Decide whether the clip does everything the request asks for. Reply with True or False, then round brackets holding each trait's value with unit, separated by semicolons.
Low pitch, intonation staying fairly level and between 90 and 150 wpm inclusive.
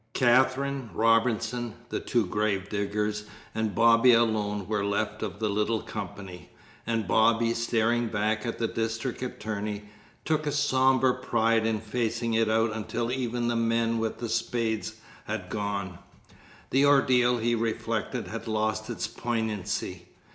True (115 Hz; 1.9 semitones; 140 wpm)